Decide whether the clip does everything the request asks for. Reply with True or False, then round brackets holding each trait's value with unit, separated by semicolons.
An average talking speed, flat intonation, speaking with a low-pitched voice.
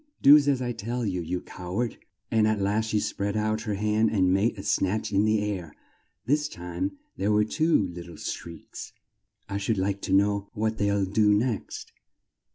True (190 wpm; 2.2 semitones; 105 Hz)